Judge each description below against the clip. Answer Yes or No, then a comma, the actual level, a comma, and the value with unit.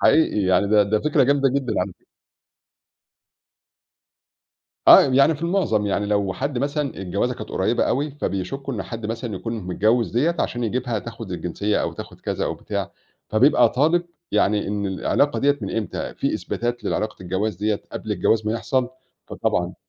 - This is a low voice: Yes, low, 115 Hz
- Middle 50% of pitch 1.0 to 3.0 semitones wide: No, average, 5.0 semitones